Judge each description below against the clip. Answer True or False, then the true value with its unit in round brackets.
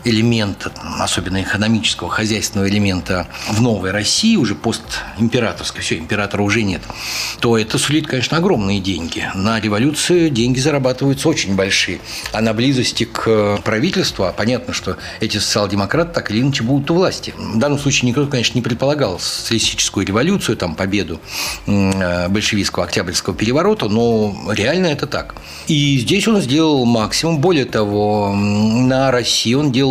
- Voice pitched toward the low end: True (115 Hz)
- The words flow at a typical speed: True (140 wpm)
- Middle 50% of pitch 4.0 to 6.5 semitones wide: True (4.6 semitones)